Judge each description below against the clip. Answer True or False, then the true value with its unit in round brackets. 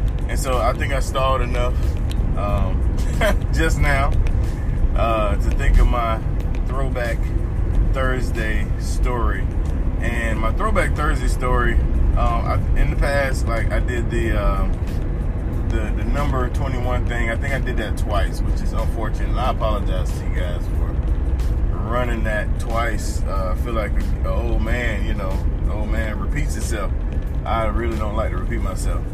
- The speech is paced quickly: False (160 wpm)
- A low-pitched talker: True (90 Hz)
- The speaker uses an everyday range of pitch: False (5.8 semitones)